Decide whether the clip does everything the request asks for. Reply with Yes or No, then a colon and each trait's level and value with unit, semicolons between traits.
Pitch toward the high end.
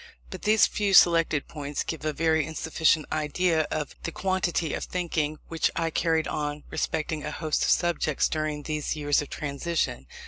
No: medium, 155 Hz